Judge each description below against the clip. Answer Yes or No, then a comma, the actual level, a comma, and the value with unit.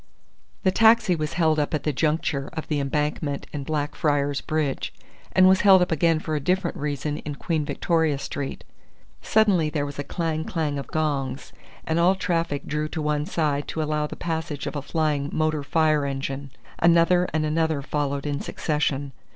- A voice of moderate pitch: Yes, medium, 155 Hz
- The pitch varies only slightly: Yes, narrow, 2.3 semitones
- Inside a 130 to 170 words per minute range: No, average, 180 wpm